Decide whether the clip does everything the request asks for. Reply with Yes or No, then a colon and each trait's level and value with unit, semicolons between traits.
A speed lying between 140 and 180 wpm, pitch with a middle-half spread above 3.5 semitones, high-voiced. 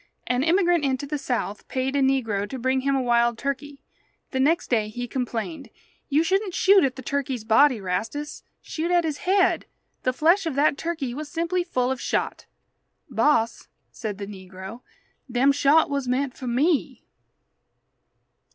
Yes: average, 165 wpm; average, 4.1 semitones; very high, 270 Hz